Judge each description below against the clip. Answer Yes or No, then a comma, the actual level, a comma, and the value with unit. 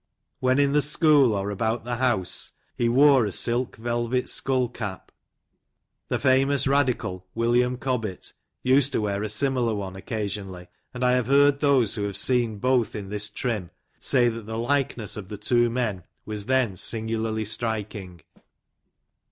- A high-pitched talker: No, low, 115 Hz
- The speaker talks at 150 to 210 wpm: Yes, average, 160 wpm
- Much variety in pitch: No, average, 3.6 semitones